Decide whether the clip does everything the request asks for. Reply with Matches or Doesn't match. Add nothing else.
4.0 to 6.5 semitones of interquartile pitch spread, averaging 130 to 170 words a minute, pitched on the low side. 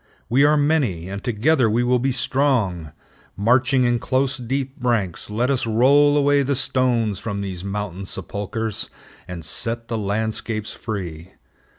Matches